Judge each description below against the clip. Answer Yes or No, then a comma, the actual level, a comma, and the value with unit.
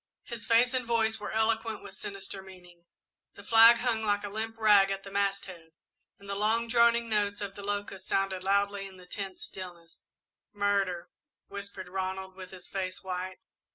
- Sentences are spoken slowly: No, average, 175 wpm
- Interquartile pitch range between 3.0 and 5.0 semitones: No, narrow, 2.6 semitones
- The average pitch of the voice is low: No, high, 200 Hz